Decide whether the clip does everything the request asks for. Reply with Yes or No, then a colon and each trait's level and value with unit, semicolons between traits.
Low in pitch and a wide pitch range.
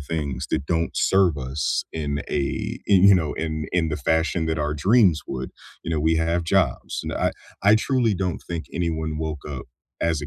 No: very low, 80 Hz; average, 2.9 semitones